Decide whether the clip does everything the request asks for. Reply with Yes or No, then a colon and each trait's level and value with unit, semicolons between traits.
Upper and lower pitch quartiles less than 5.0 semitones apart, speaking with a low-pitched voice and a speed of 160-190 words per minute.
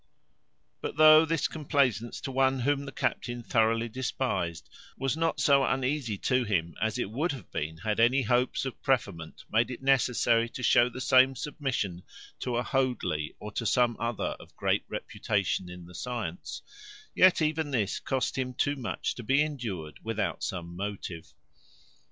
Yes: average, 4.2 semitones; low, 125 Hz; average, 165 wpm